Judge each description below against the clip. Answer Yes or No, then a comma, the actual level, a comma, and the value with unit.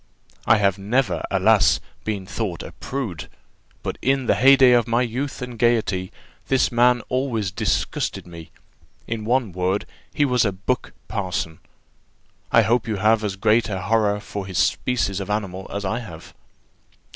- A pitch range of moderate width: Yes, average, 4.1 semitones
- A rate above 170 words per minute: No, average, 160 wpm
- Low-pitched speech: Yes, low, 110 Hz